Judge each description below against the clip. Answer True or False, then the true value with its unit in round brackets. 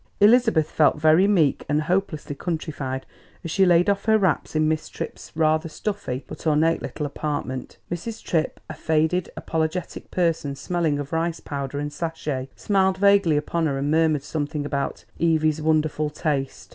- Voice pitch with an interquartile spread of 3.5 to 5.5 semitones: False (2.9 semitones)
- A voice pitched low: False (155 Hz)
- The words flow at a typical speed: True (160 wpm)